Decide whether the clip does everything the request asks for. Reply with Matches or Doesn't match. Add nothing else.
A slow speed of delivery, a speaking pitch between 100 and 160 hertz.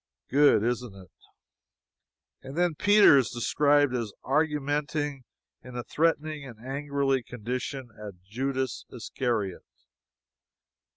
Matches